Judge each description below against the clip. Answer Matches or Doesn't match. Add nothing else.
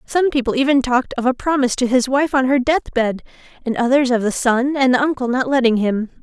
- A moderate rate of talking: Doesn't match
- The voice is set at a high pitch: Matches